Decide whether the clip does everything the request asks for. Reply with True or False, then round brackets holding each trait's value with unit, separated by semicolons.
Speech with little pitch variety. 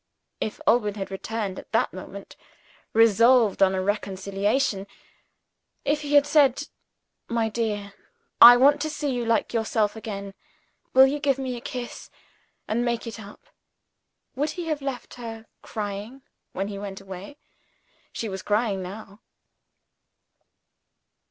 False (4.4 semitones)